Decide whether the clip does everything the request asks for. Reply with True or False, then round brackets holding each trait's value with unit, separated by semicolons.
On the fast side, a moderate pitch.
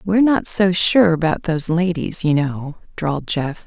False (180 wpm; 170 Hz)